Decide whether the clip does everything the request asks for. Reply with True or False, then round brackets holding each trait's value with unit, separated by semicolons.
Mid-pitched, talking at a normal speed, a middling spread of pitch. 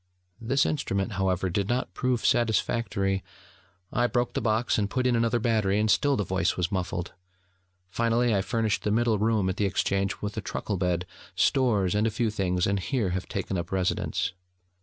False (105 Hz; 185 wpm; 3.5 semitones)